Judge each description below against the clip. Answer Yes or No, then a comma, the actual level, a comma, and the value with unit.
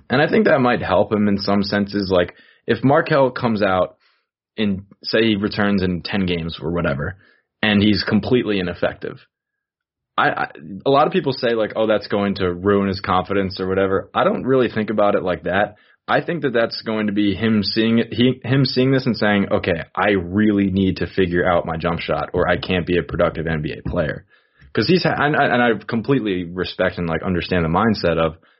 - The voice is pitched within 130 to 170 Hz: No, low, 100 Hz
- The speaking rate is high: Yes, fast, 210 wpm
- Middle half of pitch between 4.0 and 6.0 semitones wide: No, average, 3.3 semitones